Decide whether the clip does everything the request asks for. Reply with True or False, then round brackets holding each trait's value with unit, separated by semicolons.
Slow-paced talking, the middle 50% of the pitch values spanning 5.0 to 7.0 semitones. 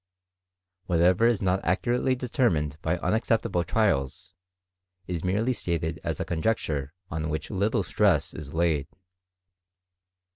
True (115 wpm; 5.5 semitones)